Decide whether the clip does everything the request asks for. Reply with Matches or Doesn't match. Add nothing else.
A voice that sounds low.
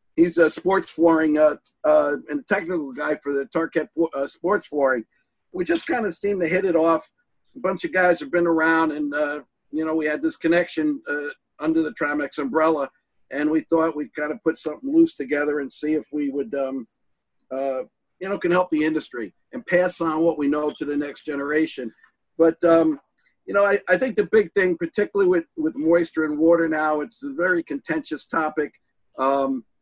Doesn't match